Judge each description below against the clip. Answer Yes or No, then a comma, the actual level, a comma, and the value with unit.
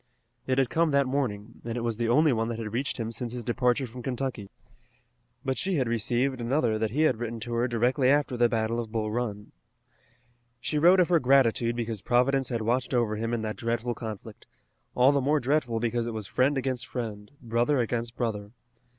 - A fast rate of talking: Yes, fast, 210 wpm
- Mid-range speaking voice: No, low, 120 Hz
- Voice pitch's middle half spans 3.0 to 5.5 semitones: No, narrow, 2.5 semitones